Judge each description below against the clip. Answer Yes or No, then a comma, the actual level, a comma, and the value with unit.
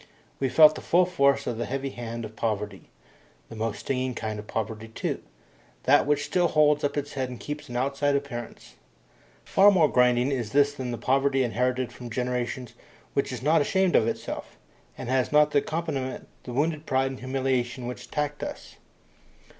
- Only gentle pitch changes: No, average, 3.1 semitones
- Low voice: Yes, low, 130 Hz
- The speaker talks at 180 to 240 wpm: Yes, average, 185 wpm